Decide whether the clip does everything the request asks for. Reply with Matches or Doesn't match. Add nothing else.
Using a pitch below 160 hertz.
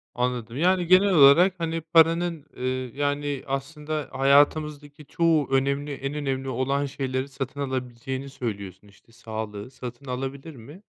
Matches